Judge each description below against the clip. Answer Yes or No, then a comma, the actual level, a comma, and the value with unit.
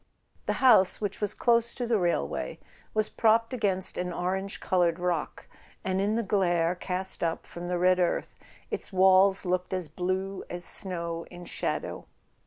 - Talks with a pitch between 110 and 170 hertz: No, medium, 185 Hz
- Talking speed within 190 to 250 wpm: No, average, 165 wpm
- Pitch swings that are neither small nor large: No, narrow, 2.2 semitones